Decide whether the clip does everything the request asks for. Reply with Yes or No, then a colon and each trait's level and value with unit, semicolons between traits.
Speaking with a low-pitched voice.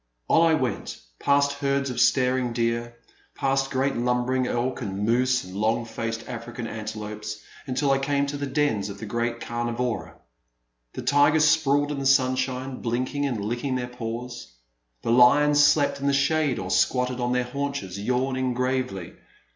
Yes: low, 125 Hz